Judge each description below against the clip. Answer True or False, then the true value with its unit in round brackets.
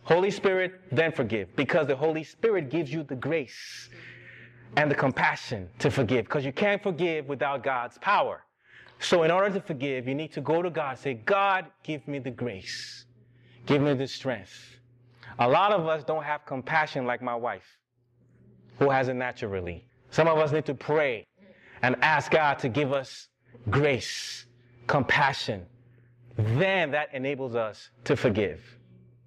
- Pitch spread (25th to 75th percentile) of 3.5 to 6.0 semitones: True (4.2 semitones)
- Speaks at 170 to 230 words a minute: False (160 wpm)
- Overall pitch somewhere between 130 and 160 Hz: True (135 Hz)